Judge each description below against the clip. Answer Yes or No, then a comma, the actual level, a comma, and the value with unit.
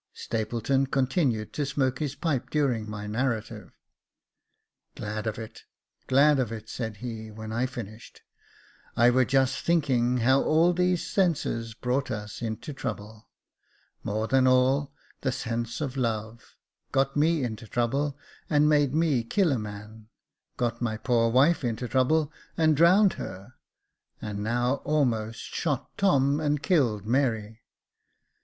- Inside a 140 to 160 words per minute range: Yes, average, 150 wpm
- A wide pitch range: No, average, 4.4 semitones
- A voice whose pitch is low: Yes, low, 125 Hz